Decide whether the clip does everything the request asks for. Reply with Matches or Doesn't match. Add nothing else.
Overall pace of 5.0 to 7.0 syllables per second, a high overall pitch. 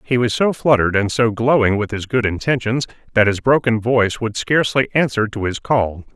Doesn't match